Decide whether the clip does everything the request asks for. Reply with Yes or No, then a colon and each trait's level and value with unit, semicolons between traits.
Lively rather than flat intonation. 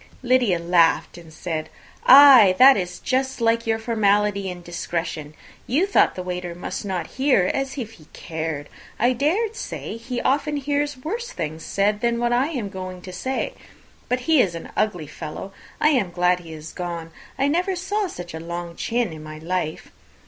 Yes: wide, 7.3 semitones